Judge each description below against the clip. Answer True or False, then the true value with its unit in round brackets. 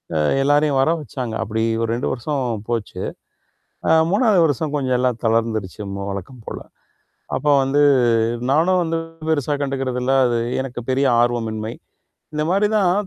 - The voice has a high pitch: False (130 Hz)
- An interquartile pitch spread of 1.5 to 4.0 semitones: False (4.6 semitones)